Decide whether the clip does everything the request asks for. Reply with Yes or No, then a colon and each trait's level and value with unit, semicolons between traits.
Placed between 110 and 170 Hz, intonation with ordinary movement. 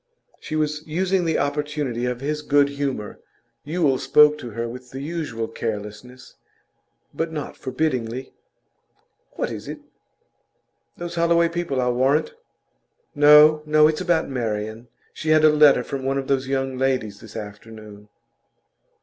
Yes: medium, 140 Hz; average, 3.9 semitones